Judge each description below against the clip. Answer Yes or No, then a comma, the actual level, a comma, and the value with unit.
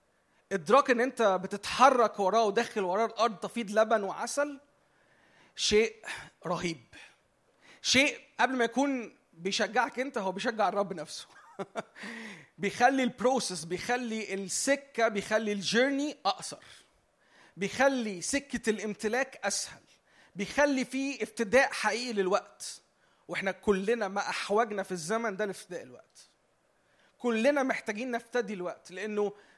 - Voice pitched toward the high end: Yes, high, 220 Hz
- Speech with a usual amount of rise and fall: Yes, average, 3.8 semitones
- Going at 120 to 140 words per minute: No, average, 110 wpm